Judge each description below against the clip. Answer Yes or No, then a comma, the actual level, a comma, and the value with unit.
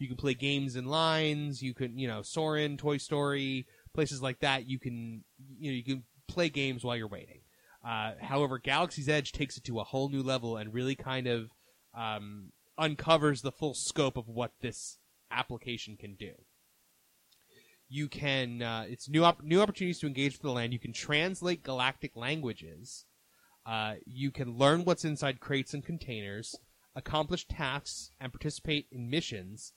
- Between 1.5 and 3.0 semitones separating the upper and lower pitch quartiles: No, average, 3.6 semitones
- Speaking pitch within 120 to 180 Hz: Yes, low, 135 Hz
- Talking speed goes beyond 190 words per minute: No, average, 175 wpm